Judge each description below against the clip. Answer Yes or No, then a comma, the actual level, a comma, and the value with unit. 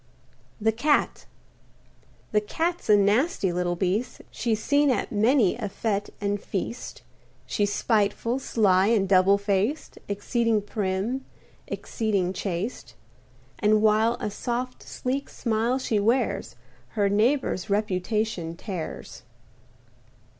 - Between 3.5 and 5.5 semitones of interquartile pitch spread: No, average, 3.1 semitones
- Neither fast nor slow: No, slow, 110 wpm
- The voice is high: Yes, high, 210 Hz